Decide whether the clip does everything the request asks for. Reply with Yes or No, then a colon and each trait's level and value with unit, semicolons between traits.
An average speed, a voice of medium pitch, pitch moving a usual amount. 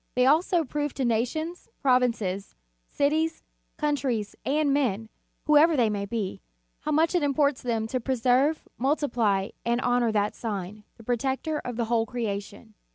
No: average, 150 wpm; very high, 250 Hz; average, 4.8 semitones